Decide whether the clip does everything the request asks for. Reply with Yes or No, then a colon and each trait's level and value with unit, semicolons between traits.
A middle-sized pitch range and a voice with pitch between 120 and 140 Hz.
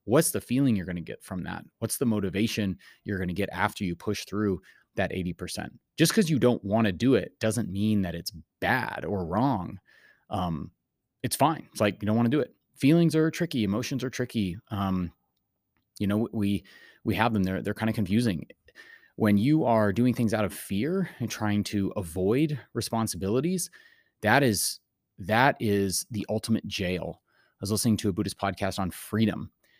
No: average, 3.1 semitones; low, 105 Hz